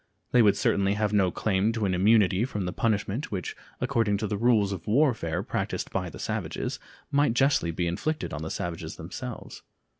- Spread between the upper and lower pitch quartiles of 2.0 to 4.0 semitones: Yes, average, 3.6 semitones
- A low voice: Yes, low, 105 Hz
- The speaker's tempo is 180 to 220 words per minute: Yes, average, 185 wpm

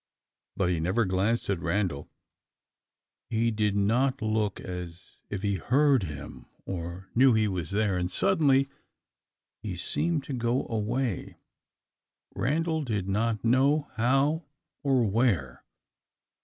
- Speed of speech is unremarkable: No, slow, 125 wpm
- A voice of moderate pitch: No, low, 110 Hz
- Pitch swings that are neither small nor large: No, wide, 5.7 semitones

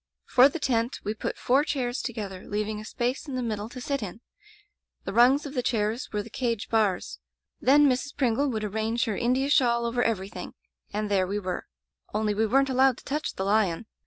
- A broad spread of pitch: No, average, 3.6 semitones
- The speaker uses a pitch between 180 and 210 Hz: No, high, 235 Hz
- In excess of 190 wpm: Yes, fast, 205 wpm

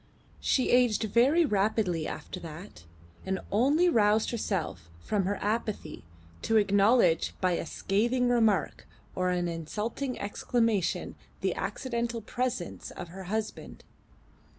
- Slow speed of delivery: Yes, slow, 120 wpm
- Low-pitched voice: No, high, 210 Hz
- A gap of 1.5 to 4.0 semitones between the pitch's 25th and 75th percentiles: No, average, 4.5 semitones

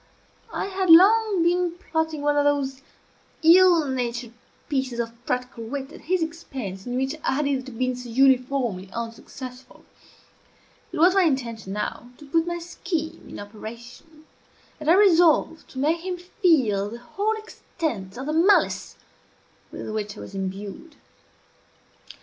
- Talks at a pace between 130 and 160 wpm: Yes, average, 150 wpm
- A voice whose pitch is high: Yes, very high, 280 Hz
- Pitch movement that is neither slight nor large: No, wide, 5.9 semitones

